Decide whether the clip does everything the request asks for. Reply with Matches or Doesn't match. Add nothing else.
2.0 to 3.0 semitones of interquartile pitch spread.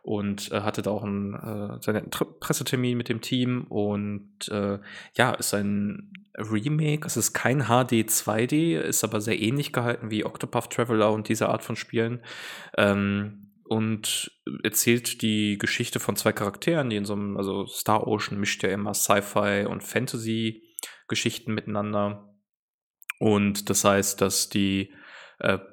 Matches